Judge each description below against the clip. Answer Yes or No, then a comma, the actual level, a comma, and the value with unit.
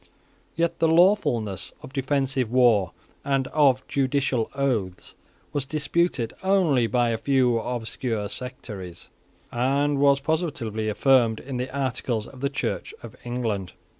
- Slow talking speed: Yes, slow, 130 wpm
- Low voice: Yes, low, 130 Hz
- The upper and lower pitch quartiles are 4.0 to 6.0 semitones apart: No, average, 3.6 semitones